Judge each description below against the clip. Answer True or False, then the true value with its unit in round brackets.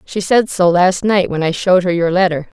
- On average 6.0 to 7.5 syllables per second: False (5.3 syllables/s)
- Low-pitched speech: False (180 Hz)